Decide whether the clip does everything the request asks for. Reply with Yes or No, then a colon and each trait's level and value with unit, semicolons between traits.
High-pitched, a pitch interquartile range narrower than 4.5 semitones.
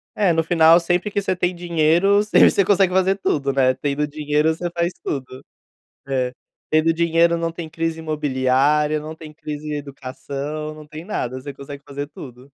No: medium, 155 Hz; average, 3.1 semitones